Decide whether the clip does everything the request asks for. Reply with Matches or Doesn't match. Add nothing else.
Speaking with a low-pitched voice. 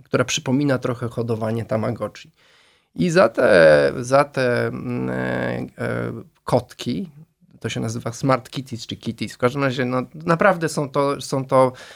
Matches